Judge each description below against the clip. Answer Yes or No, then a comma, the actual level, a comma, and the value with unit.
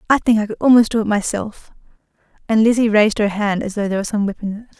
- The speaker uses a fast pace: Yes, fast, 265 wpm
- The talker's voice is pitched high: Yes, high, 215 Hz